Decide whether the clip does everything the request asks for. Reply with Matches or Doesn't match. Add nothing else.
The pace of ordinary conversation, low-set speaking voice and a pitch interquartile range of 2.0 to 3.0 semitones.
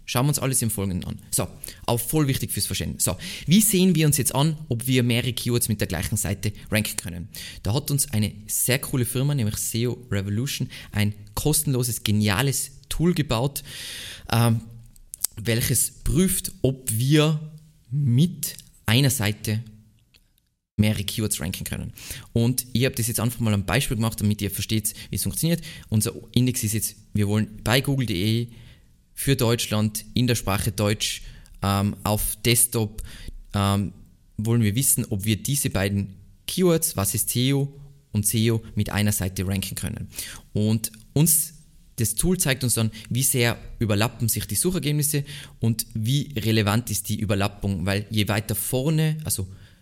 Doesn't match